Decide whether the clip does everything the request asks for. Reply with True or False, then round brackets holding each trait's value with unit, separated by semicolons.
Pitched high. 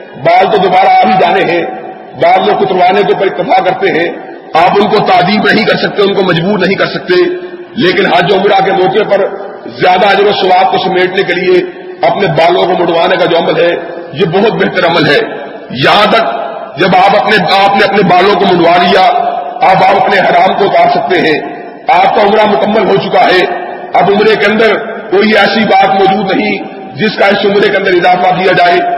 True (195 Hz)